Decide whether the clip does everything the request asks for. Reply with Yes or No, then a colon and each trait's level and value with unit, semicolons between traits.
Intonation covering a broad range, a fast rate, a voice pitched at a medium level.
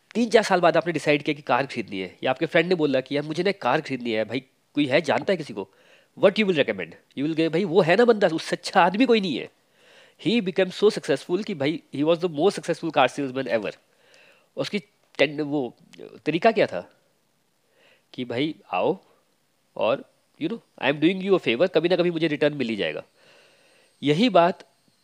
Yes: wide, 5.9 semitones; fast, 205 wpm; medium, 170 Hz